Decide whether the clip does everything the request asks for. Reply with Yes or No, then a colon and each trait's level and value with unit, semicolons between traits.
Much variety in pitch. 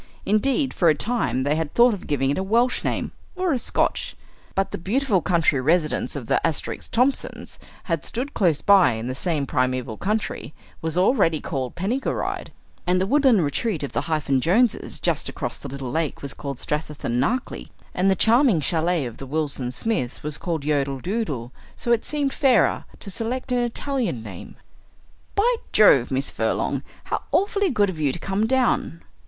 Yes: wide, 8.6 semitones